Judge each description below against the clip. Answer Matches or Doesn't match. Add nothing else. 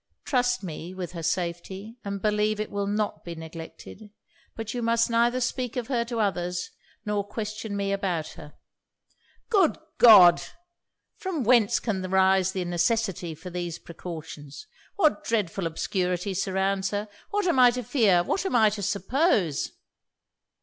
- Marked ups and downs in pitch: Doesn't match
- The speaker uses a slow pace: Doesn't match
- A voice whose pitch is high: Matches